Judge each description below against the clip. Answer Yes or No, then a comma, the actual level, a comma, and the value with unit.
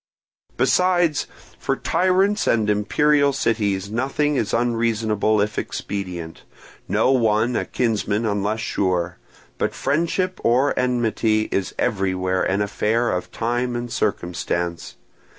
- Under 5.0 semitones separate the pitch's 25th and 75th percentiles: Yes, average, 4.1 semitones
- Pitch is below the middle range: Yes, low, 110 Hz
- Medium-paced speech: No, slow, 115 wpm